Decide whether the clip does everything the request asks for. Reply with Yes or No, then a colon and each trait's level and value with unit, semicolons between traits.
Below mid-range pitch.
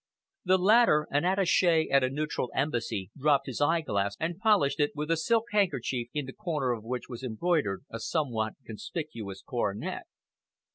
No: medium, 145 Hz